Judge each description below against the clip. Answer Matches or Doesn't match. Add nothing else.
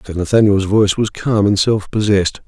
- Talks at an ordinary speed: Matches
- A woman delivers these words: Doesn't match